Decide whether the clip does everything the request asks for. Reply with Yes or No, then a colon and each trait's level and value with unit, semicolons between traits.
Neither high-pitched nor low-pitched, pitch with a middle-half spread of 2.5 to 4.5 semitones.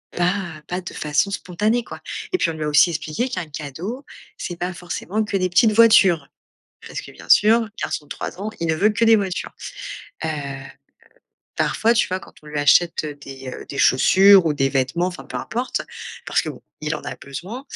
No: medium, 180 Hz; wide, 5.5 semitones